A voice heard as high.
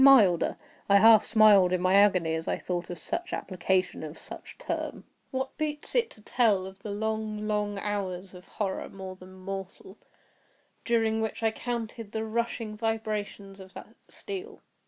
Yes: high, 210 Hz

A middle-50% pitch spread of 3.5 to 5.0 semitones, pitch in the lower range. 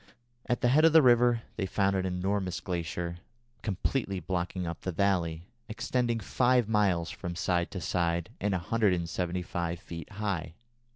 Yes: average, 3.9 semitones; very low, 95 Hz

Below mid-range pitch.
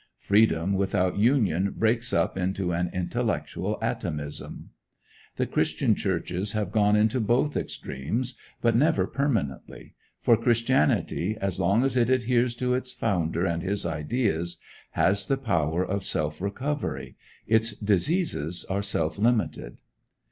Yes: low, 100 Hz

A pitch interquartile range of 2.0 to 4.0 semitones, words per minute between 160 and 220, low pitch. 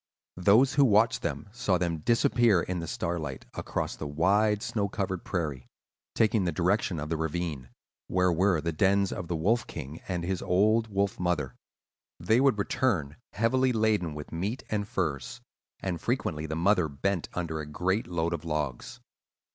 No: average, 4.6 semitones; average, 170 wpm; very low, 90 Hz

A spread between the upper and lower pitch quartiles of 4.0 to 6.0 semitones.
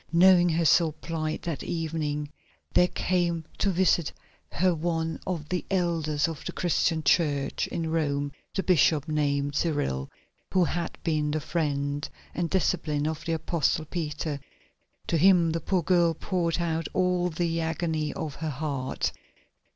No: narrow, 2.4 semitones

